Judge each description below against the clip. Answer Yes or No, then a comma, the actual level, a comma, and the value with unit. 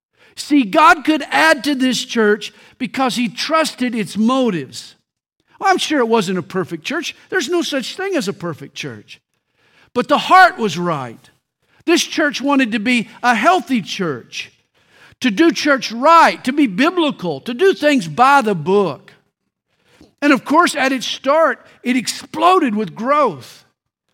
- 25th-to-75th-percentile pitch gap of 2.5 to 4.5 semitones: No, wide, 5.5 semitones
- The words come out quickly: No, average, 155 wpm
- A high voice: Yes, very high, 265 Hz